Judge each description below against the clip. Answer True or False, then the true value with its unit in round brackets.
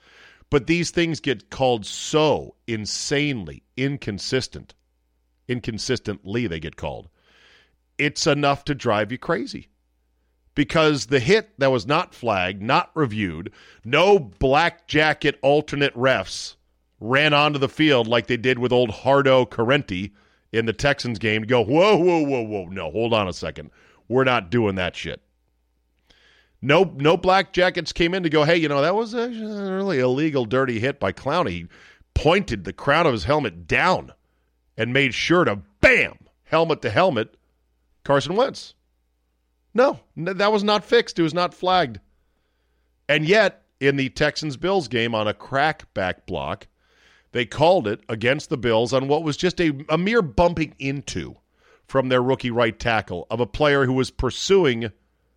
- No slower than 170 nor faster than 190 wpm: False (160 wpm)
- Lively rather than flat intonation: True (7.9 semitones)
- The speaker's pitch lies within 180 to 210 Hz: False (130 Hz)